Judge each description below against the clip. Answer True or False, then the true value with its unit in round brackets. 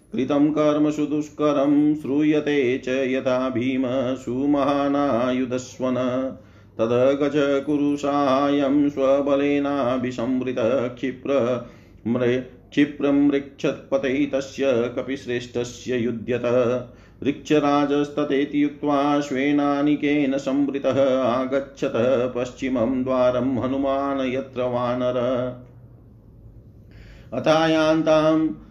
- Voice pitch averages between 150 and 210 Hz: False (135 Hz)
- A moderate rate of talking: False (55 wpm)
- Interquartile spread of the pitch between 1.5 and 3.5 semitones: True (2.4 semitones)